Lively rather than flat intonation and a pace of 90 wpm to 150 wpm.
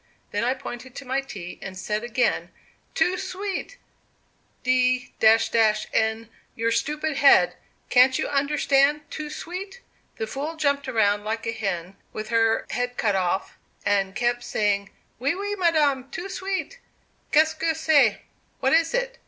Yes: wide, 6.0 semitones; average, 145 wpm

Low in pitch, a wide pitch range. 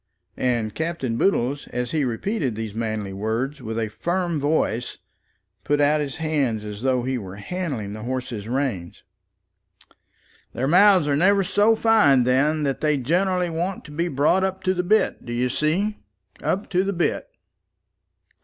No: medium, 145 Hz; wide, 6.9 semitones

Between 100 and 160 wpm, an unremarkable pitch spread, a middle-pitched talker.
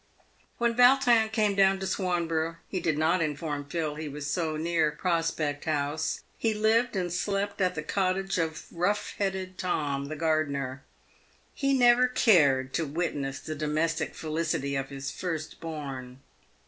Yes: average, 155 wpm; average, 4.6 semitones; medium, 165 Hz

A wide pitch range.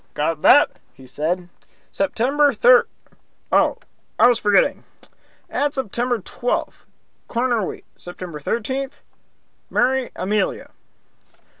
Yes: wide, 6.4 semitones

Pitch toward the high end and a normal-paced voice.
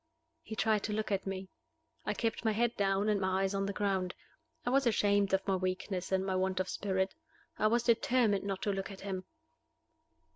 No: high, 195 Hz; fast, 210 wpm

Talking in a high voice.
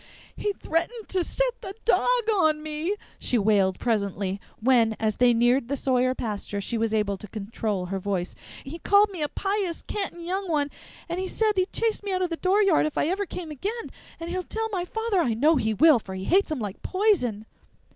Yes: very high, 310 Hz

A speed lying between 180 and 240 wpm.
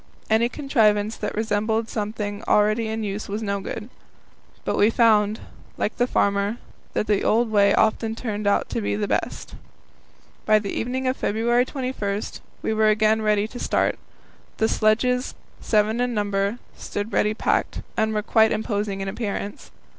No: average, 160 wpm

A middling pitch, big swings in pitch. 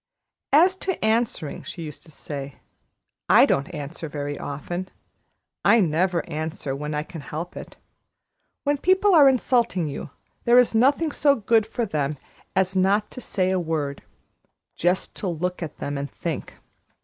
Yes: medium, 180 Hz; wide, 7.5 semitones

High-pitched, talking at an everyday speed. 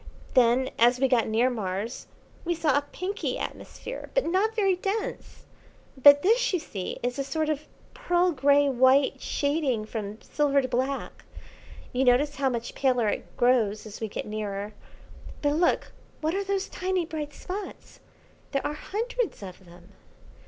Yes: very high, 275 Hz; average, 160 wpm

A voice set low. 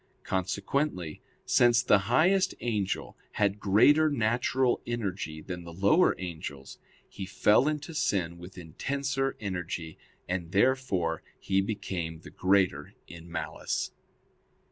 Yes: low, 100 Hz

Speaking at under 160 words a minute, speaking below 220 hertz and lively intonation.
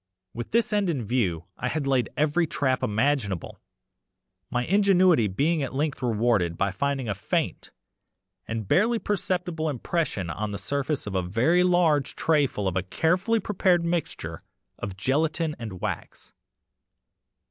Yes: average, 145 wpm; medium, 140 Hz; wide, 8.0 semitones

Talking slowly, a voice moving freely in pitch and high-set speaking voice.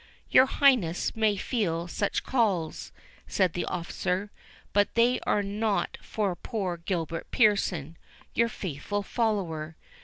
No: slow, 120 wpm; average, 4.3 semitones; high, 200 Hz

